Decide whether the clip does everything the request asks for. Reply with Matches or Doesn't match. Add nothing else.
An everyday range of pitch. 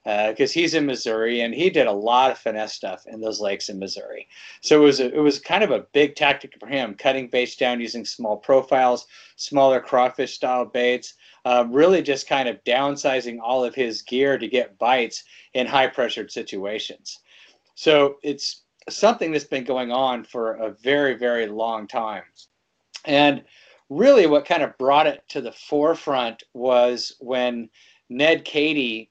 Matches